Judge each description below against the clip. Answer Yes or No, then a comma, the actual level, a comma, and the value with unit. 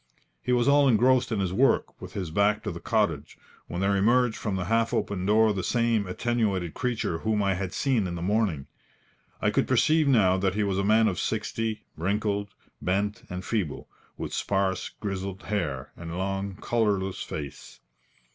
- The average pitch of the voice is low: Yes, low, 100 Hz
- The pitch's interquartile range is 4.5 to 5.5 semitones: No, average, 3.1 semitones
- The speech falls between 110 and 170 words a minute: No, average, 180 wpm